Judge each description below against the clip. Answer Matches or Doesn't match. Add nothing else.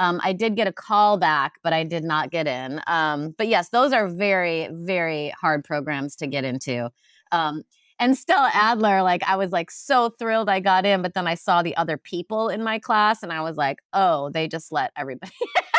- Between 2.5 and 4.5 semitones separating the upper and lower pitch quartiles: Doesn't match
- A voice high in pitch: Doesn't match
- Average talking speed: Doesn't match